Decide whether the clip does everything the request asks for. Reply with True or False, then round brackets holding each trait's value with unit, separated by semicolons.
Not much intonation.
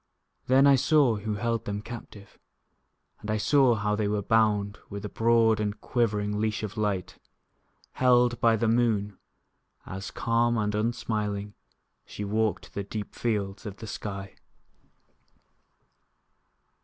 True (2.2 semitones)